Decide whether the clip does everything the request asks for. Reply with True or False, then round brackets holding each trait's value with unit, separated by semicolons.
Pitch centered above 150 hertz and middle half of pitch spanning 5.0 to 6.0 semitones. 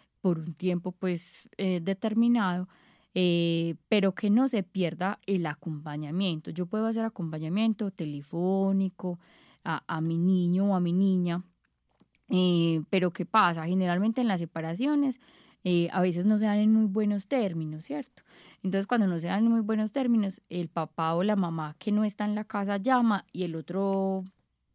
False (185 Hz; 3.6 semitones)